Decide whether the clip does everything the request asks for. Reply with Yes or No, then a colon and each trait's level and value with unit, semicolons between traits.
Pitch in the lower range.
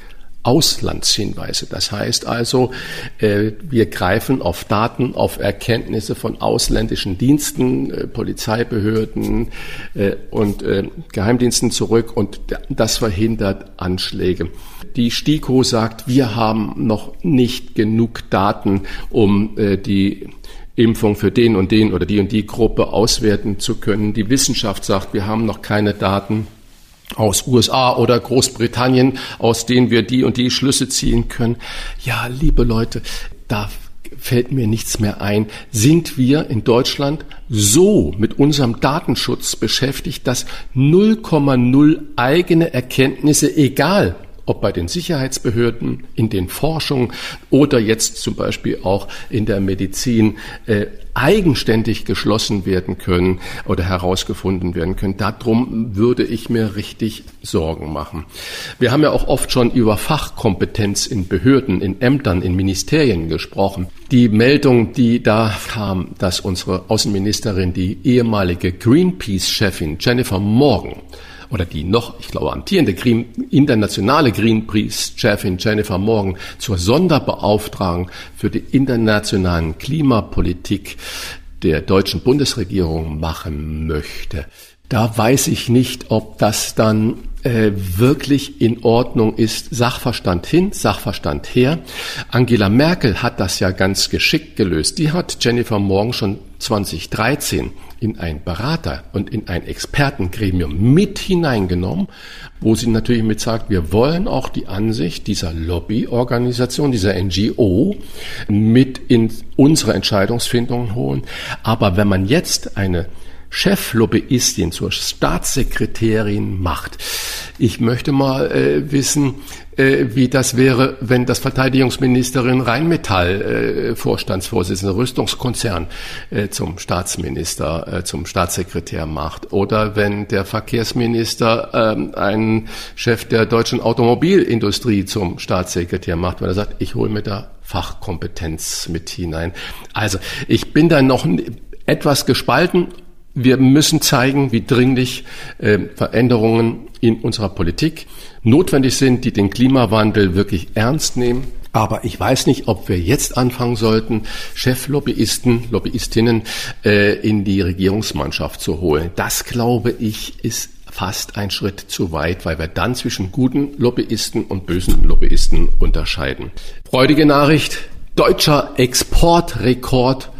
Yes: low, 110 Hz